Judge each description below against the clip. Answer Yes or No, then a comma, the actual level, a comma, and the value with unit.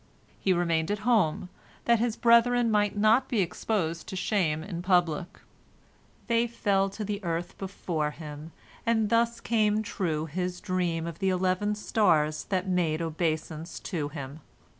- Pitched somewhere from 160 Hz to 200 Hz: Yes, medium, 185 Hz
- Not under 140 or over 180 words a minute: Yes, average, 150 wpm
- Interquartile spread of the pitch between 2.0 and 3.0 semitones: No, average, 4.5 semitones